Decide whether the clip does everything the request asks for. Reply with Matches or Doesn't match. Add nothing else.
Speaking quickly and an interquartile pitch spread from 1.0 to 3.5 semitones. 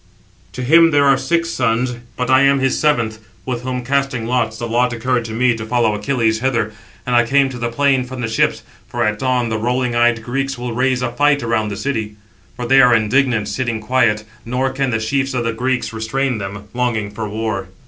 Matches